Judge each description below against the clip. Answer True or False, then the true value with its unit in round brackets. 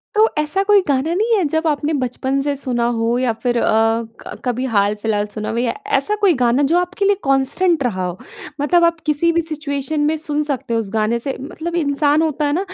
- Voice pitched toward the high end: True (285 Hz)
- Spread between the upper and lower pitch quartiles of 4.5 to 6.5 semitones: True (5.3 semitones)